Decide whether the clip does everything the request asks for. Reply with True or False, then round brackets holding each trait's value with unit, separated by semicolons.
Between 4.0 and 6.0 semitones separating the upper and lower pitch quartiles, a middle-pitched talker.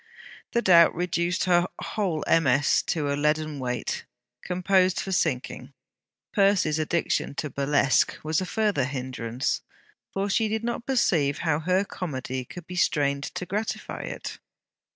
True (4.8 semitones; 165 Hz)